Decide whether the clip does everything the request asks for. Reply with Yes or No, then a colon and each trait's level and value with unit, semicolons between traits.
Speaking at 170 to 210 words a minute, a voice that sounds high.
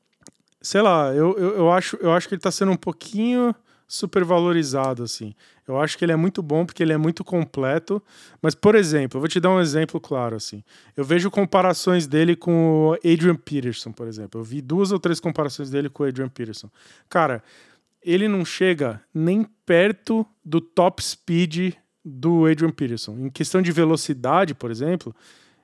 No: fast, 185 wpm; medium, 165 Hz